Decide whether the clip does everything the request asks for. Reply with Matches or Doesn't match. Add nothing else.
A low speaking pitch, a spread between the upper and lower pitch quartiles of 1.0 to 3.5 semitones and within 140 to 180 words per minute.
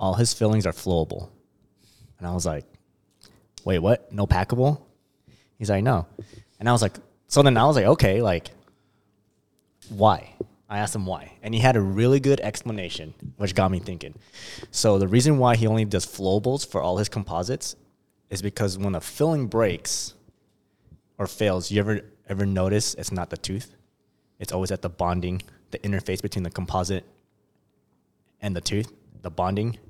Matches